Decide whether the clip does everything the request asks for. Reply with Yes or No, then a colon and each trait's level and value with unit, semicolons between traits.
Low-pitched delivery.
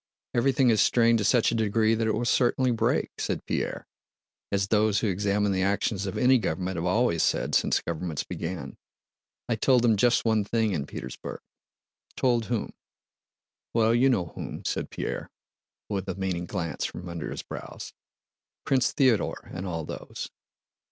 Yes: low, 105 Hz